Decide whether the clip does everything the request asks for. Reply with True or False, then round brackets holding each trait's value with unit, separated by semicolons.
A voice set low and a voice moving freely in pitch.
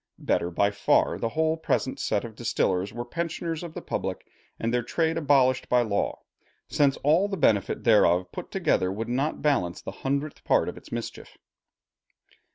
True (125 Hz; 6.7 semitones)